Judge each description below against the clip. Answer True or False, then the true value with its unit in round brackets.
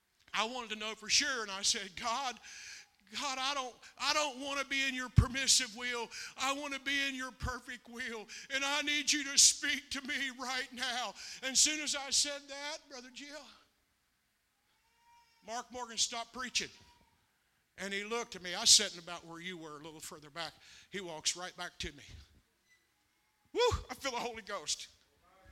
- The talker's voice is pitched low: False (255 Hz)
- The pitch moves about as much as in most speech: True (4.7 semitones)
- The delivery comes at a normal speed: True (190 wpm)